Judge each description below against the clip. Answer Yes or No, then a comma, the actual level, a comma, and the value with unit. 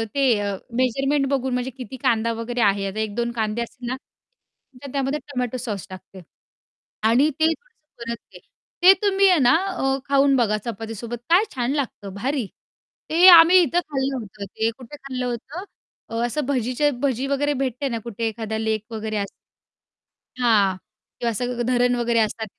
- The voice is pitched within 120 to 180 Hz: No, high, 245 Hz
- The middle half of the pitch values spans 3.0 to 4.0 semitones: Yes, average, 3.7 semitones